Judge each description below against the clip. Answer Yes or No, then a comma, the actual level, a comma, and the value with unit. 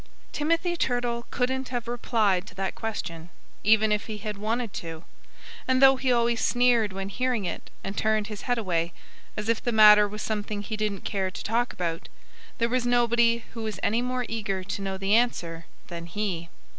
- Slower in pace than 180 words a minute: No, average, 190 wpm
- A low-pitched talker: No, high, 215 Hz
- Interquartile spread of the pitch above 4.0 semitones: No, average, 3.6 semitones